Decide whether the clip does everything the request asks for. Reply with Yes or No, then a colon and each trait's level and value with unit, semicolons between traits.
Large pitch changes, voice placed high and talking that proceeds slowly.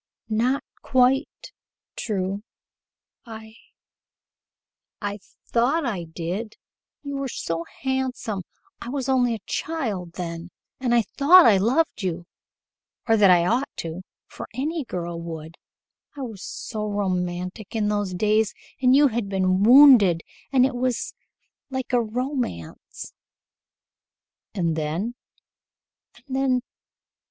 Yes: wide, 5.9 semitones; high, 220 Hz; slow, 120 wpm